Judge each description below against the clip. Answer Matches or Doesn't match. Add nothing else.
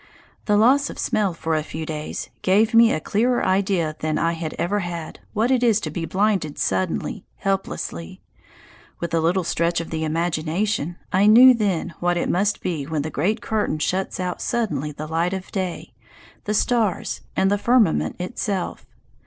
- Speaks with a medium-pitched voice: Matches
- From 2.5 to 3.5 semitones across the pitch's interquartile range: Doesn't match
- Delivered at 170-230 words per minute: Matches